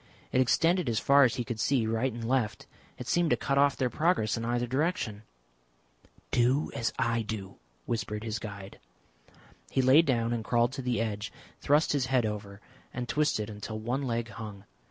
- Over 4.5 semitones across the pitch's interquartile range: No, average, 3.4 semitones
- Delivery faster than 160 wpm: Yes, average, 185 wpm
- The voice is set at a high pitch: No, low, 120 Hz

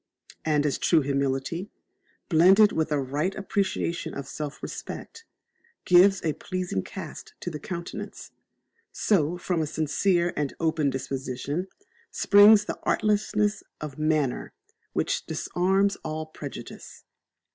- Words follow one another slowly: Yes, slow, 120 wpm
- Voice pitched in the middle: Yes, medium, 160 Hz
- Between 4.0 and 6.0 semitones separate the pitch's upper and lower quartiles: Yes, average, 4.6 semitones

